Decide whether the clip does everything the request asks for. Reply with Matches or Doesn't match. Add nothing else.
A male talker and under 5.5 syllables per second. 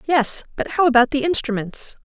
Doesn't match